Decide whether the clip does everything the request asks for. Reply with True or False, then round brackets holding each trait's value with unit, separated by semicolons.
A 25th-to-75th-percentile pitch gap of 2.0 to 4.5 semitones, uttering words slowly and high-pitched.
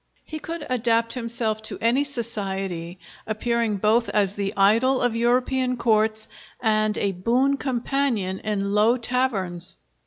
True (3.5 semitones; 130 wpm; 230 Hz)